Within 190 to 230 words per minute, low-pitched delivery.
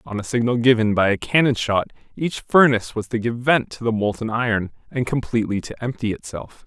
Yes: fast, 205 wpm; low, 115 Hz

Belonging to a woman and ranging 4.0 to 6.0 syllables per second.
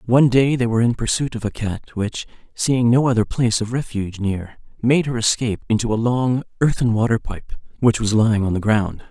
No: male; 5.6 syllables/s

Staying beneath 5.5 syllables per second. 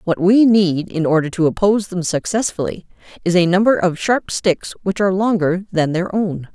Yes: 5.2 syllables/s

